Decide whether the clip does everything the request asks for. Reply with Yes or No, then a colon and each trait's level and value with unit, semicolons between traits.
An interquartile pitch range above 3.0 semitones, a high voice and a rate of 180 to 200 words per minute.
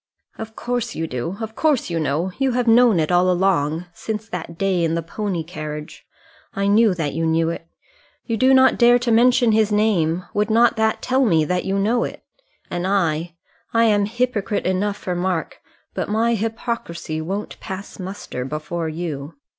Yes: average, 5.1 semitones; high, 195 Hz; average, 185 wpm